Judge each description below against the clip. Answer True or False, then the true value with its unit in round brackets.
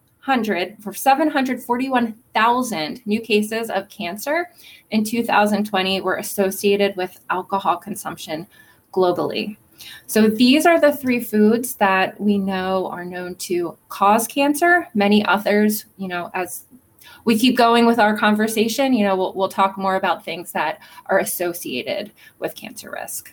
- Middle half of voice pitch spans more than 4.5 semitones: False (3.8 semitones)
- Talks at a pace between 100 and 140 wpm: True (135 wpm)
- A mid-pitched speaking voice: False (210 Hz)